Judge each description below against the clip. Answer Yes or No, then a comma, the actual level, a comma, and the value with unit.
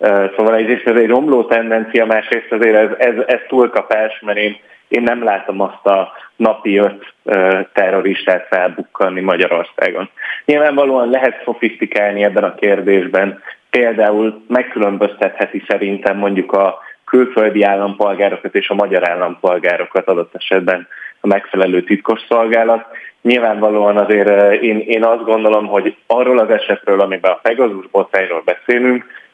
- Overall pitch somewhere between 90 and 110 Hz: Yes, low, 105 Hz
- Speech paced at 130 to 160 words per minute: No, average, 120 wpm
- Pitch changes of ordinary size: No, narrow, 2.3 semitones